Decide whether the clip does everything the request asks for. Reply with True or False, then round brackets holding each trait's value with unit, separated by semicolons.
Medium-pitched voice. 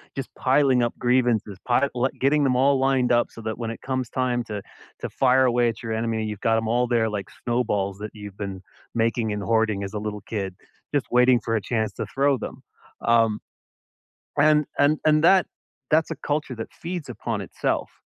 False (120 Hz)